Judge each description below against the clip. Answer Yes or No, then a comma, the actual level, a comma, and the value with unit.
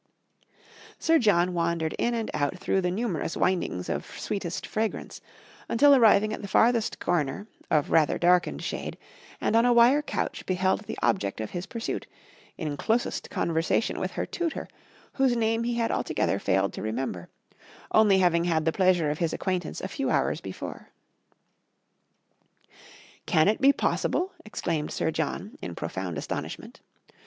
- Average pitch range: No, wide, 6.0 semitones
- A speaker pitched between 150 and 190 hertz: Yes, medium, 185 Hz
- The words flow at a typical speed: Yes, average, 155 wpm